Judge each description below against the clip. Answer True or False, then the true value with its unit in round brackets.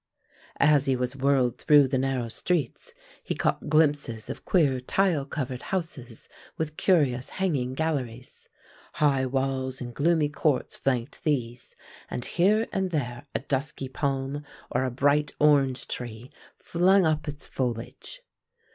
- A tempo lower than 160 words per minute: True (140 wpm)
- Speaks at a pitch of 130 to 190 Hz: True (140 Hz)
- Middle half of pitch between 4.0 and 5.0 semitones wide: False (3.3 semitones)